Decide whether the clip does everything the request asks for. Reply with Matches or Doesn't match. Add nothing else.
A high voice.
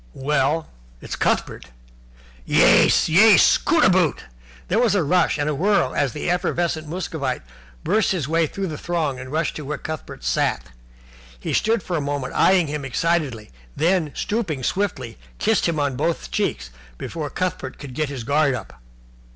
Doesn't match